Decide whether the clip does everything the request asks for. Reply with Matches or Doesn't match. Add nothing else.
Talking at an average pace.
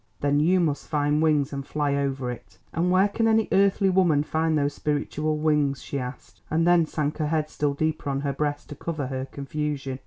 Doesn't match